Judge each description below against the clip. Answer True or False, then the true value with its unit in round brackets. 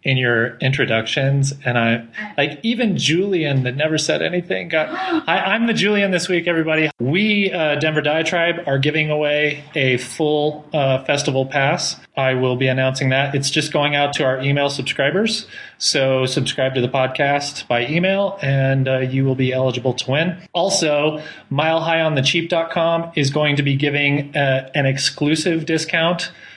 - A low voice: False (145 Hz)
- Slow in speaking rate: False (170 wpm)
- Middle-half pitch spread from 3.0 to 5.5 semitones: True (3.7 semitones)